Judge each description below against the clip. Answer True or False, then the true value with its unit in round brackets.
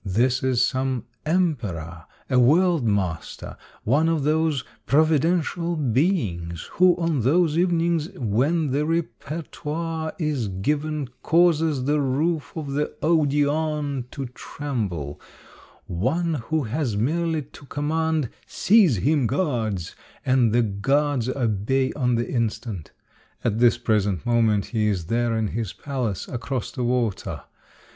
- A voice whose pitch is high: False (135 Hz)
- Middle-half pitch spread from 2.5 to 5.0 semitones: False (5.6 semitones)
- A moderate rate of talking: False (130 wpm)